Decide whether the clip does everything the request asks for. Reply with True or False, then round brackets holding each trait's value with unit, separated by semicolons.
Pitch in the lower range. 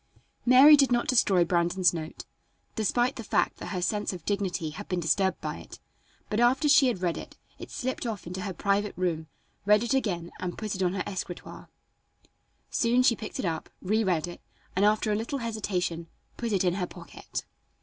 False (200 Hz)